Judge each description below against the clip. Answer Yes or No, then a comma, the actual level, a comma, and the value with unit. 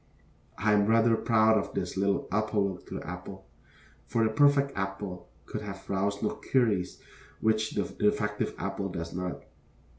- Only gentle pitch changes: Yes, narrow, 2.1 semitones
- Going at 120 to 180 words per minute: Yes, average, 155 wpm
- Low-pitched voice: Yes, low, 105 Hz